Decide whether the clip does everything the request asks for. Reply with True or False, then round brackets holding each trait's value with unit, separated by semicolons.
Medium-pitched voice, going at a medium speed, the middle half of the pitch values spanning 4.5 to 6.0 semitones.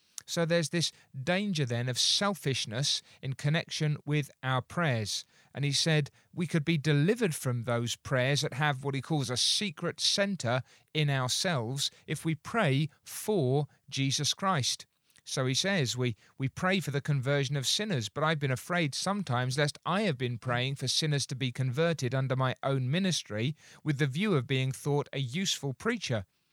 False (145 Hz; 175 wpm; 4.1 semitones)